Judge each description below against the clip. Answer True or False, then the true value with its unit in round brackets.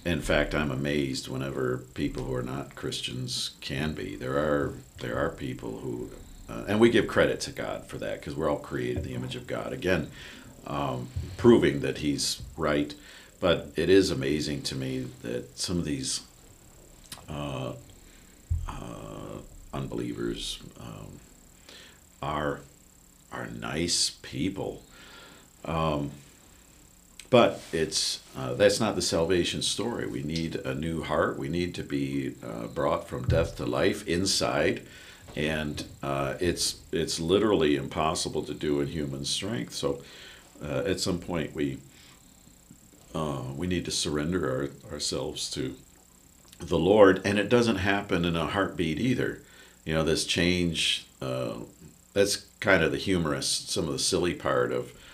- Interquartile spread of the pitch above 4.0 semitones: True (4.4 semitones)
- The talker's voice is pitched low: True (75 Hz)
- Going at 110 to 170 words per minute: True (150 wpm)